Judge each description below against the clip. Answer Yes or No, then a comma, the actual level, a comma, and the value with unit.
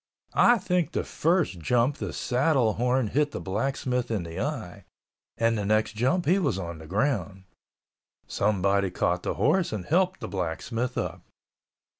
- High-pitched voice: No, low, 115 Hz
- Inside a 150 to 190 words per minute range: Yes, average, 160 wpm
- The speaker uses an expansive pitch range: Yes, wide, 6.8 semitones